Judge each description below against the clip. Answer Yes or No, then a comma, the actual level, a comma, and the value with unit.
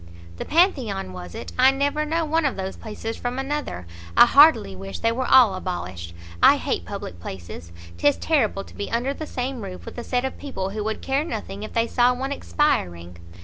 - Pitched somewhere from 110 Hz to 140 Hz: No, high, 230 Hz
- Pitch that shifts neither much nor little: No, wide, 6.9 semitones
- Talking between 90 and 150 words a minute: No, fast, 205 wpm